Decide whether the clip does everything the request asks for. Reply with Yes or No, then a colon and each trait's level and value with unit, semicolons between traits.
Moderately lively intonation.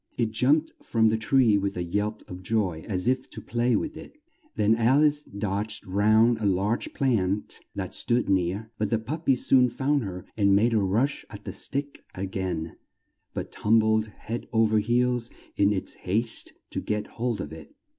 Yes: average, 3.3 semitones